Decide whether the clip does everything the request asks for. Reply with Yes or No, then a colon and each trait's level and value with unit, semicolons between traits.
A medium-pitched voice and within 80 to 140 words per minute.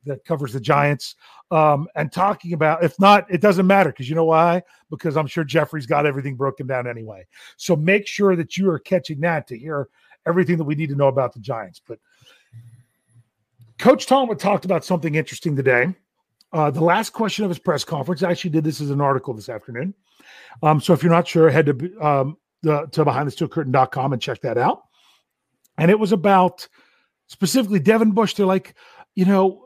No: medium, 160 Hz; average, 195 wpm